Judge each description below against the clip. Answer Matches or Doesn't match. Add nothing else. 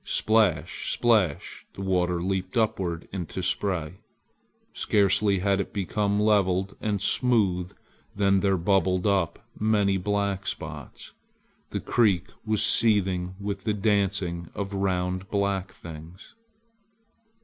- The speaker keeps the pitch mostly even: Matches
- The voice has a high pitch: Doesn't match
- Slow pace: Matches